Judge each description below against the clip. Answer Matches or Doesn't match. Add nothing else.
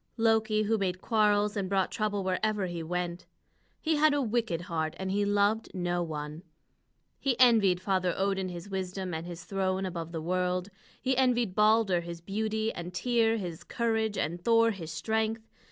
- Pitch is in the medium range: Doesn't match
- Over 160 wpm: Matches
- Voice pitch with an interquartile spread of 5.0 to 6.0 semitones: Doesn't match